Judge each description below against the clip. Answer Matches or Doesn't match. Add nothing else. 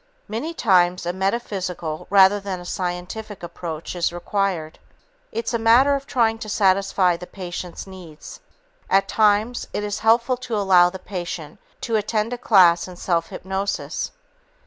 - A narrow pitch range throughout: Doesn't match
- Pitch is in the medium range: Doesn't match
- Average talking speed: Matches